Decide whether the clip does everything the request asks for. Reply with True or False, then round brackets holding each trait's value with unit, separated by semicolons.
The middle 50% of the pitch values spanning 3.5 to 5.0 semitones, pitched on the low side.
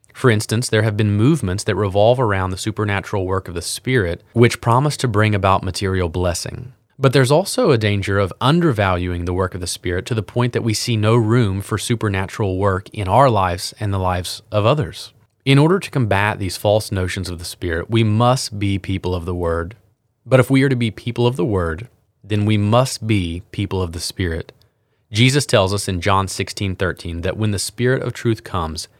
True (4.2 semitones; 105 Hz)